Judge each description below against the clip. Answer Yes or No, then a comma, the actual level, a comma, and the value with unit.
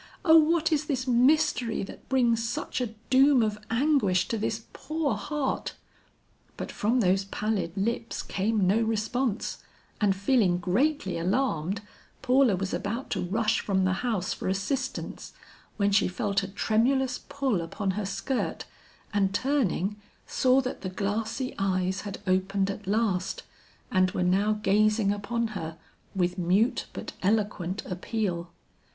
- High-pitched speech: Yes, high, 210 Hz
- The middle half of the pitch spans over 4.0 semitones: Yes, average, 4.6 semitones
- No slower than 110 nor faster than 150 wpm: Yes, average, 145 wpm